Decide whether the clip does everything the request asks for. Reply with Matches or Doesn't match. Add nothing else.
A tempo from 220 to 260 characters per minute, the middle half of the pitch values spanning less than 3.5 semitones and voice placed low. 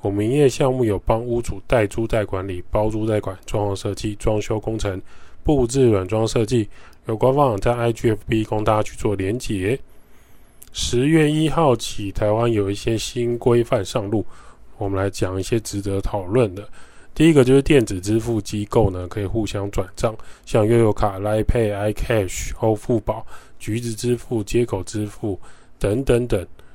Doesn't match